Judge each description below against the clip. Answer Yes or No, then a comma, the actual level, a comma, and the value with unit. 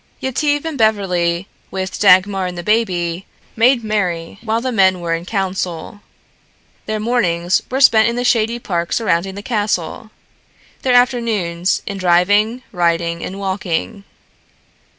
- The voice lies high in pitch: Yes, high, 200 Hz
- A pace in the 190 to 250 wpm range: No, slow, 135 wpm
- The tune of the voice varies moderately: Yes, average, 4.5 semitones